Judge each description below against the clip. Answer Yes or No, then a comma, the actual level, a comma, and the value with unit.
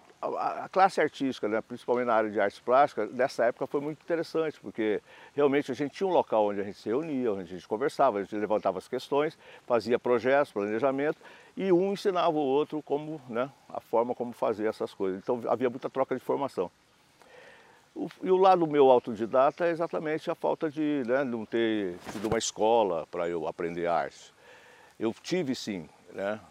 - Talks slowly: No, fast, 185 wpm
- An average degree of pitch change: No, wide, 6.1 semitones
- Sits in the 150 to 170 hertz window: No, low, 135 Hz